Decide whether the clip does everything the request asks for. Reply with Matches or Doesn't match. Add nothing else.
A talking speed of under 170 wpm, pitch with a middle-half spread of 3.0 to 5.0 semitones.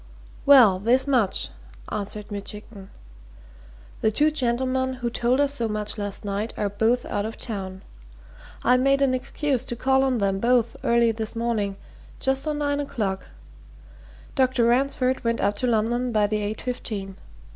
Matches